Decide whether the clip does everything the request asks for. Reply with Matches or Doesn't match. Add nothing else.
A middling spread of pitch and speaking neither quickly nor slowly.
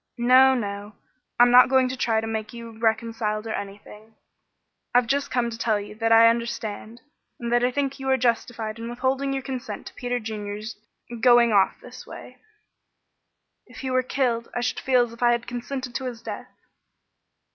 Doesn't match